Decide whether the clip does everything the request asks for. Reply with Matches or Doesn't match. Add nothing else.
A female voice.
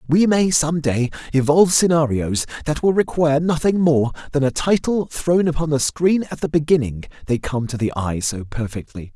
Doesn't match